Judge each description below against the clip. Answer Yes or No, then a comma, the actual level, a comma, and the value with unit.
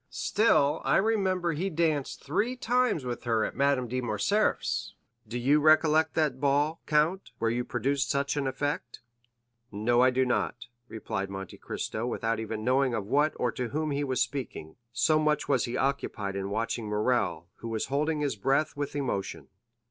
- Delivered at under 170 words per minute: No, average, 180 wpm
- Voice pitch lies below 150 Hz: Yes, low, 135 Hz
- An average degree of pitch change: Yes, average, 4.6 semitones